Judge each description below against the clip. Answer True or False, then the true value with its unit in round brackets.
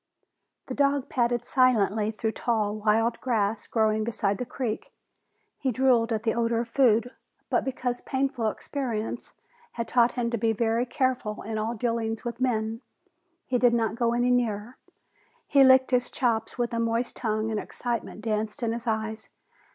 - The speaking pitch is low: False (230 Hz)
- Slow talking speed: False (165 wpm)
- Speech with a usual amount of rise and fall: False (2.0 semitones)